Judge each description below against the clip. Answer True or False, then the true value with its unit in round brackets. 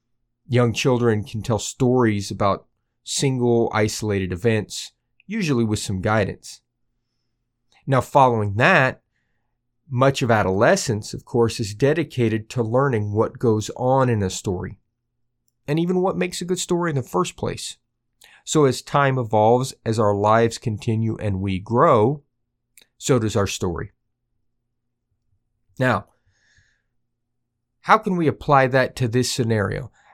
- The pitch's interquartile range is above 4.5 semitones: False (2.8 semitones)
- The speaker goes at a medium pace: False (130 wpm)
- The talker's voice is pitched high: False (120 Hz)